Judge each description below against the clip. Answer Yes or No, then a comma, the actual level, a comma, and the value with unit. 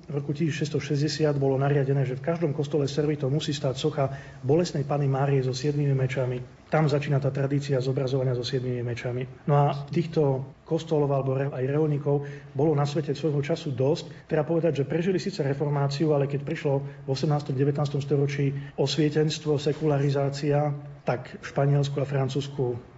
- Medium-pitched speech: Yes, medium, 145 Hz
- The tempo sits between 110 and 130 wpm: No, average, 160 wpm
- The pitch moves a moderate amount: No, narrow, 1.8 semitones